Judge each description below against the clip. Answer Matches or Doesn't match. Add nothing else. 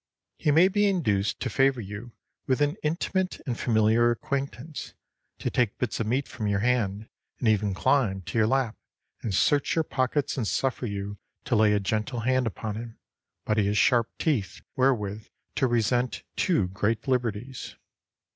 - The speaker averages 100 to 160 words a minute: Doesn't match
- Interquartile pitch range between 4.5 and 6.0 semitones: Doesn't match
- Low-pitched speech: Matches